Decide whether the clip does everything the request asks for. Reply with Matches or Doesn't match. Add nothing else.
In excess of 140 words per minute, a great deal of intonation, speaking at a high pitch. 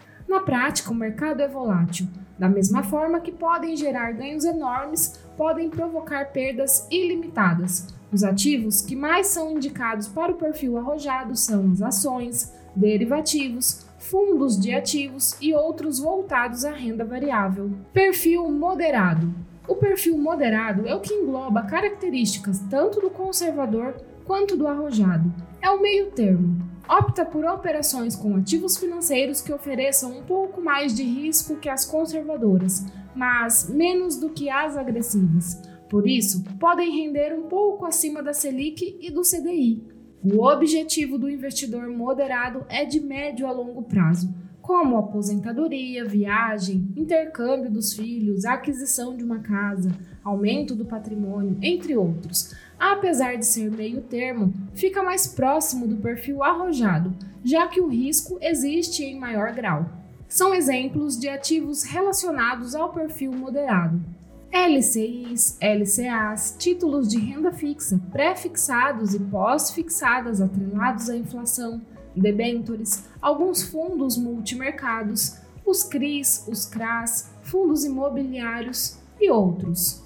Doesn't match